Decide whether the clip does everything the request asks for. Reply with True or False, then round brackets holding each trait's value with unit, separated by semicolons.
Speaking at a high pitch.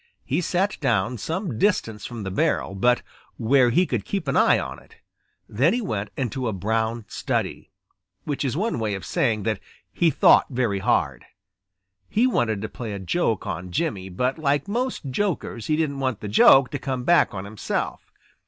False (125 Hz)